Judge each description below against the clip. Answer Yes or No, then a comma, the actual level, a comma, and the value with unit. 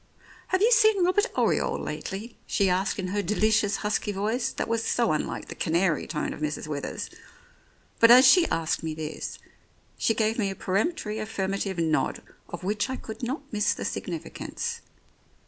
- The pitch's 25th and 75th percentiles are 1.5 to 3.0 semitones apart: No, average, 4.5 semitones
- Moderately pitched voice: No, high, 210 Hz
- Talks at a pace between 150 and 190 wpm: Yes, average, 175 wpm